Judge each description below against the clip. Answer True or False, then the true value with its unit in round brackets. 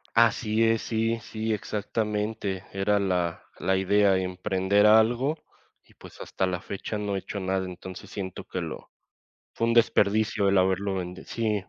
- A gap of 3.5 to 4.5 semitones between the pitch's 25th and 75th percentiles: False (2.7 semitones)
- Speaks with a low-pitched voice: True (100 Hz)